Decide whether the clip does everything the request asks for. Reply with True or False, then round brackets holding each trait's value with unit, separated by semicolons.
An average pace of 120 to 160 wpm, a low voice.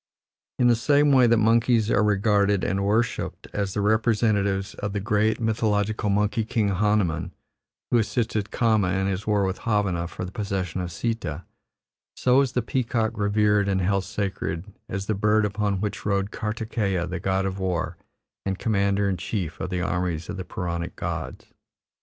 False (170 wpm; 100 Hz)